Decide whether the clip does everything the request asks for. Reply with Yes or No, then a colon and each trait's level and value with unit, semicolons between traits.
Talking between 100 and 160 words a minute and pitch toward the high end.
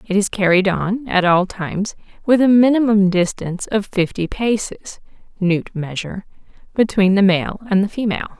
Yes: average, 155 wpm; high, 200 Hz